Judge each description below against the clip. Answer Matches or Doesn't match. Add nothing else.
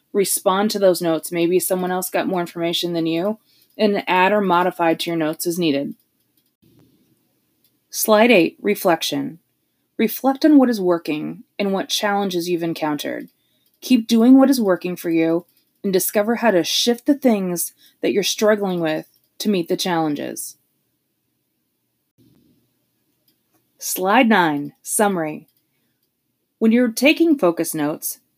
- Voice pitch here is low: Doesn't match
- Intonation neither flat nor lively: Matches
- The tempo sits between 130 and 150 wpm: Matches